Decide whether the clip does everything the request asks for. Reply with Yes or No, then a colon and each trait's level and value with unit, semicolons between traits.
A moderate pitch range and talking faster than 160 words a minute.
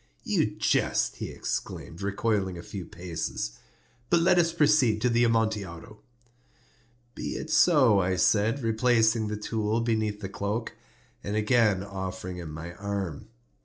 No: average, 3.4 semitones; average, 140 wpm